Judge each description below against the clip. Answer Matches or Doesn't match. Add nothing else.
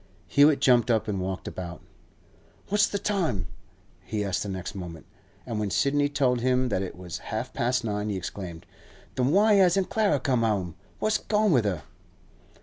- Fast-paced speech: Doesn't match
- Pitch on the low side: Matches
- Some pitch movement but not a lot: Doesn't match